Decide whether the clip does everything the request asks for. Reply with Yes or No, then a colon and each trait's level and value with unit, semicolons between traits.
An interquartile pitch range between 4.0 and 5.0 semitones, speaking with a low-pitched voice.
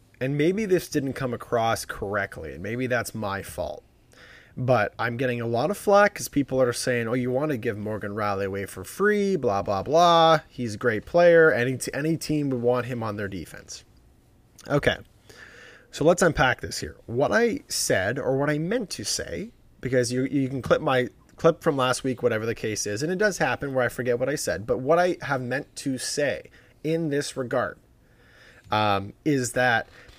Yes: average, 4.7 semitones; low, 125 Hz